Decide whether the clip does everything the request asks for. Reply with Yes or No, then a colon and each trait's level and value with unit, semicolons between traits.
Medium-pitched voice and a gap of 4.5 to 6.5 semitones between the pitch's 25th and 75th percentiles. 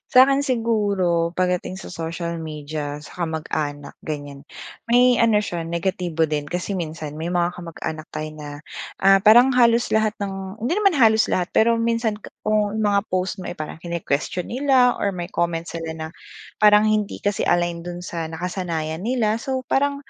Yes: medium, 180 Hz; average, 5.0 semitones